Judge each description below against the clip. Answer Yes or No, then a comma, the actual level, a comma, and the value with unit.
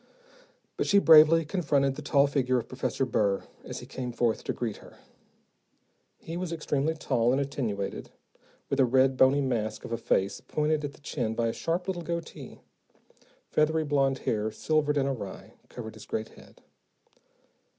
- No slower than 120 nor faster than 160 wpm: No, average, 170 wpm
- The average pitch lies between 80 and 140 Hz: Yes, low, 135 Hz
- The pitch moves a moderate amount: Yes, average, 4.5 semitones